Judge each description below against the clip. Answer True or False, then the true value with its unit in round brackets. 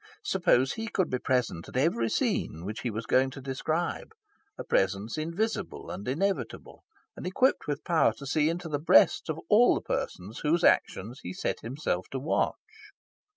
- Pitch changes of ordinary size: False (6.5 semitones)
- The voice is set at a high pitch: False (140 Hz)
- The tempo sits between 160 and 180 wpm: True (175 wpm)